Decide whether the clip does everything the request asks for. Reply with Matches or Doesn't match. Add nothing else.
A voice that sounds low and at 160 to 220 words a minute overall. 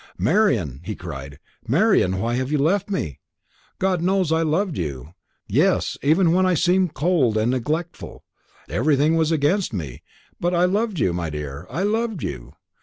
Doesn't match